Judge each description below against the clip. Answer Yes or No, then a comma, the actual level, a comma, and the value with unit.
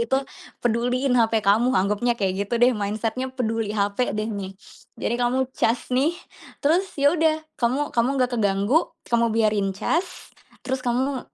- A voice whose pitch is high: Yes, high, 235 Hz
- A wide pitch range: No, average, 3.6 semitones